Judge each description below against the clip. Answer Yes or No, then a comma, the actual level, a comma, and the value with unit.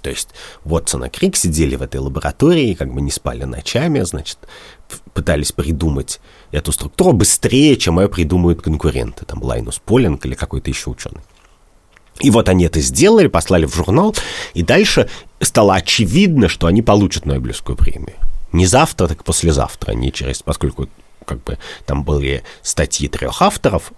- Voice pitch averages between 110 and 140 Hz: No, very low, 80 Hz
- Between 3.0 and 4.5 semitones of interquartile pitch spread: No, average, 4.9 semitones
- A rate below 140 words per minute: No, fast, 160 wpm